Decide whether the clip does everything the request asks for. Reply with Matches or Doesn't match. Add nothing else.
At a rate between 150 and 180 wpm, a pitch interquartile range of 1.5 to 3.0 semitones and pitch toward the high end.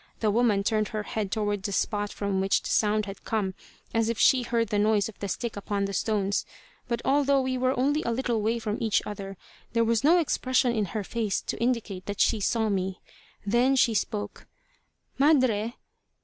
Doesn't match